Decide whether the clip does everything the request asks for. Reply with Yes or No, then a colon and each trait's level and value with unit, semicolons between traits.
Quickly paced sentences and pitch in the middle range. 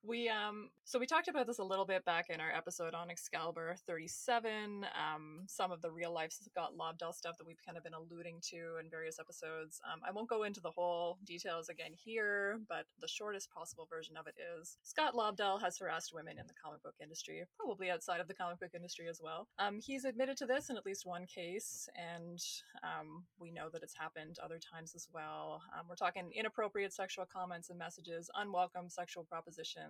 Yes: fast, 210 wpm; medium, 175 Hz